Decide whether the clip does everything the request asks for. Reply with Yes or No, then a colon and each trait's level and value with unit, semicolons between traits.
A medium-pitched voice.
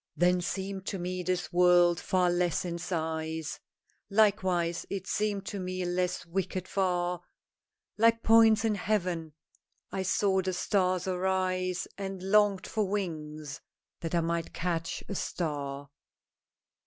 Yes: medium, 180 Hz